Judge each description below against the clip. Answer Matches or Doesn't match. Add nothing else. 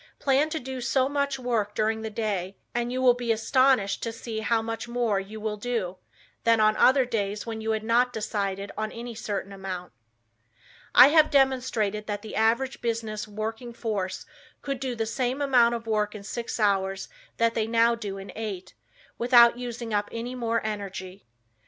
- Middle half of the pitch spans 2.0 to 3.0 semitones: Matches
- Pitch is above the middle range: Matches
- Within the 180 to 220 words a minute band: Matches